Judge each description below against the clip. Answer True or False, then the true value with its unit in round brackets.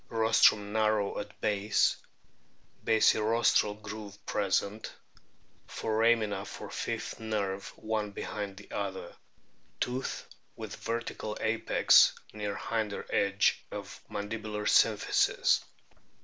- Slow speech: True (90 wpm)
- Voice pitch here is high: False (105 Hz)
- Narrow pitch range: True (1.5 semitones)